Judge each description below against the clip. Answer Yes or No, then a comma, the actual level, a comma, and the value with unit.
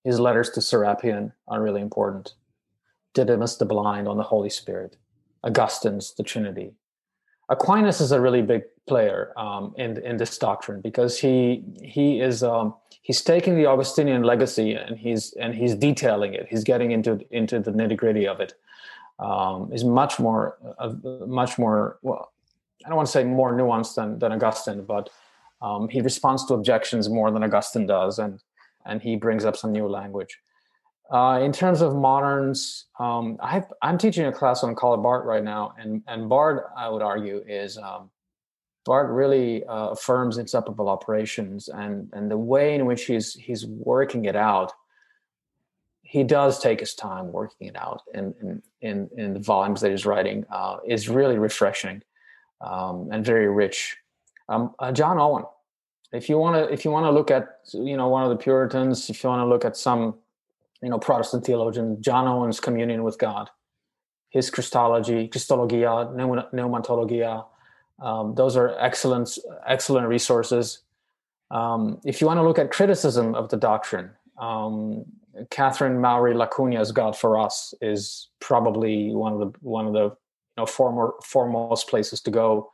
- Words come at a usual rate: Yes, average, 170 wpm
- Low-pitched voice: Yes, low, 120 Hz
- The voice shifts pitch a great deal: No, average, 3.3 semitones